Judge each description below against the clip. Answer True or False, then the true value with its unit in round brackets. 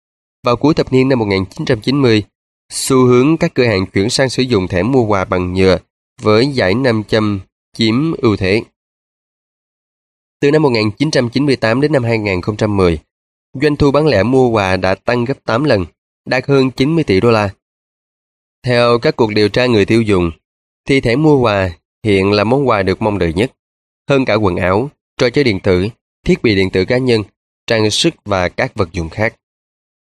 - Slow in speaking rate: False (180 wpm)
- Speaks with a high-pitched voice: False (115 Hz)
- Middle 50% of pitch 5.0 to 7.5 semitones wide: True (5.4 semitones)